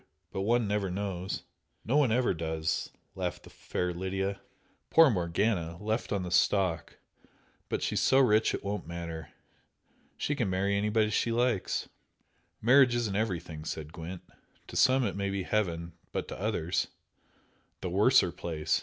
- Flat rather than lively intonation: No, average, 4.3 semitones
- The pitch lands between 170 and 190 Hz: No, low, 100 Hz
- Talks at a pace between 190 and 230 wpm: No, average, 160 wpm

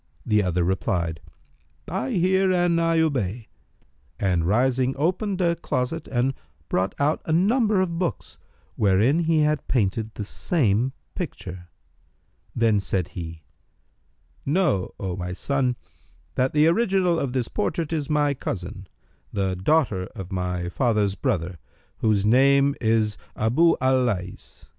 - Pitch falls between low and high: No, low, 125 Hz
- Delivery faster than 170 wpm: No, slow, 135 wpm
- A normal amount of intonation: No, wide, 9.0 semitones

